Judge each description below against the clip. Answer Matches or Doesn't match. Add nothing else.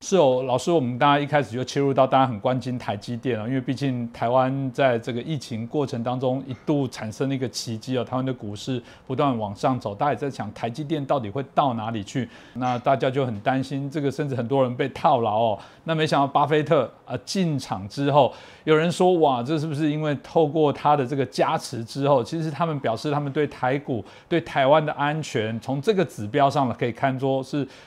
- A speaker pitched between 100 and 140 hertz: Matches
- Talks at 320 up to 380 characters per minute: Matches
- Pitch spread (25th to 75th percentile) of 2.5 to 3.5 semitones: Matches